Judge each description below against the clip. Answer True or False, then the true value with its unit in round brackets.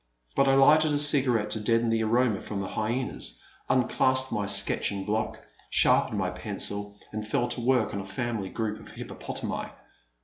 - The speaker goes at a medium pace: True (170 wpm)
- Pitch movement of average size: True (3.9 semitones)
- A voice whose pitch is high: False (110 Hz)